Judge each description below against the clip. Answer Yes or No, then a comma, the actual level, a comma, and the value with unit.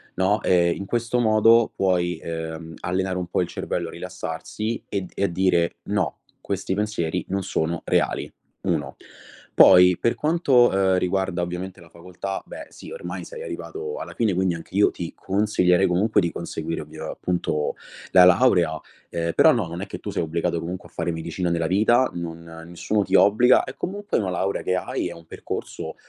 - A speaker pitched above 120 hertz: No, very low, 90 Hz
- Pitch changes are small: No, average, 3.3 semitones